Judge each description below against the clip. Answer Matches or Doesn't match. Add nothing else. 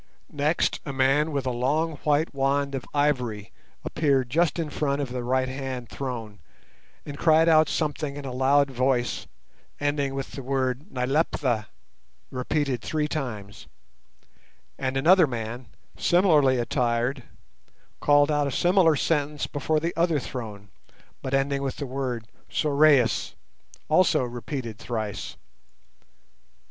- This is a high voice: Doesn't match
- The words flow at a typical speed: Doesn't match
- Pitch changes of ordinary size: Matches